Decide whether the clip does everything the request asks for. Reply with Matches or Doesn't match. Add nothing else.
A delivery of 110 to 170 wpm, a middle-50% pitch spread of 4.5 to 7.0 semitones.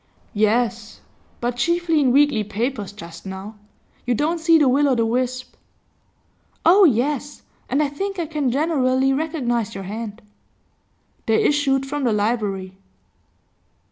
Matches